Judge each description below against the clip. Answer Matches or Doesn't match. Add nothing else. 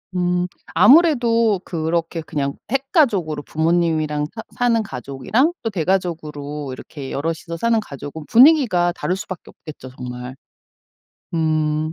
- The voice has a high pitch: Doesn't match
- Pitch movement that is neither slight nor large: Doesn't match